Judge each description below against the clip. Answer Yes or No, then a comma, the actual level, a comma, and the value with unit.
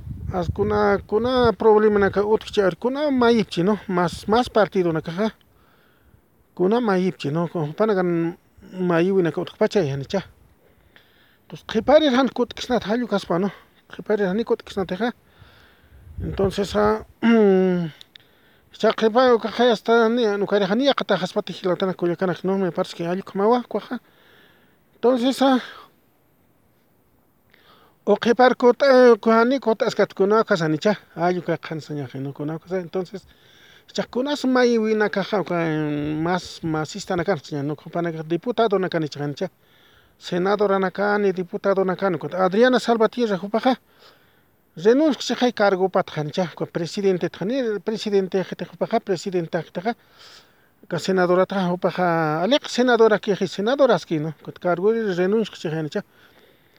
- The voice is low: No, high, 195 Hz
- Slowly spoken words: Yes, slow, 90 wpm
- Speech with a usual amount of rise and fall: Yes, average, 4.1 semitones